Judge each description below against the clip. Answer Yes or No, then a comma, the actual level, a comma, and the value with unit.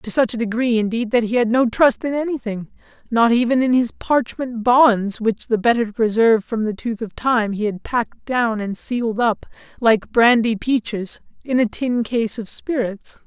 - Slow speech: No, average, 200 wpm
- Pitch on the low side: No, high, 230 Hz